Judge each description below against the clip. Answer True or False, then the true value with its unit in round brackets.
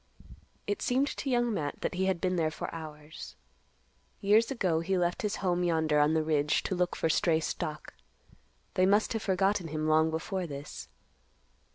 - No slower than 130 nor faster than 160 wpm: False (180 wpm)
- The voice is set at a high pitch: False (175 Hz)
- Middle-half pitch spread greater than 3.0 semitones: True (3.7 semitones)